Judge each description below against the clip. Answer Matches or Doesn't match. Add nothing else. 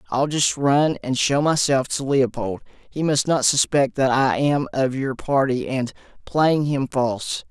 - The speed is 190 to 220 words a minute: Doesn't match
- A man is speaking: Matches